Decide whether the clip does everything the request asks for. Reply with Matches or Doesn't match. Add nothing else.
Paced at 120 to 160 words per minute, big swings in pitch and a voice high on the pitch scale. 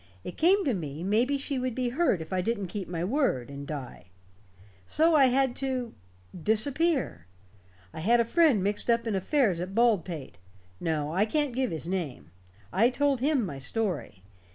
Doesn't match